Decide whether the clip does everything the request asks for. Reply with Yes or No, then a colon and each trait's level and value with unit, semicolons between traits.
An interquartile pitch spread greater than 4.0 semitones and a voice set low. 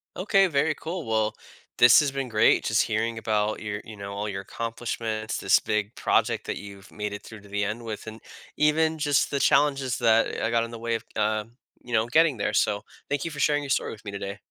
Yes: average, 4.7 semitones; low, 115 Hz